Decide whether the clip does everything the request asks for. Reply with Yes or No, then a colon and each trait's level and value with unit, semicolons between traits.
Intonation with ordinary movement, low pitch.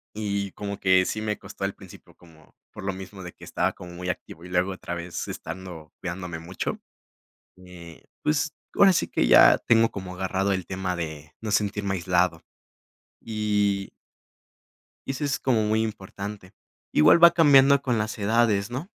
Yes: average, 3.3 semitones; very low, 95 Hz